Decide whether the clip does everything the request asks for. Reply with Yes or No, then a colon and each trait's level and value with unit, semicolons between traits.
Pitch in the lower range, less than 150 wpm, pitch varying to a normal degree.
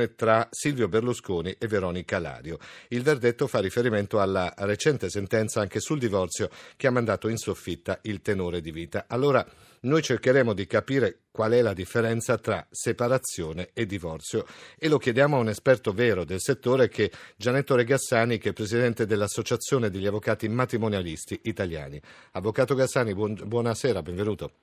No: low, 110 Hz; average, 155 wpm; average, 3.5 semitones